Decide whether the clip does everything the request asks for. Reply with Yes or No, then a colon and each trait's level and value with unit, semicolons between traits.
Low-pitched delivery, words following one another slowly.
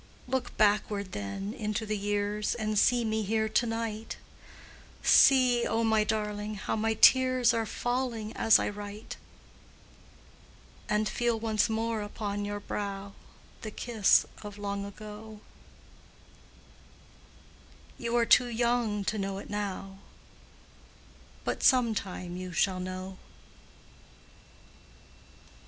No: high, 215 Hz; slow, 115 wpm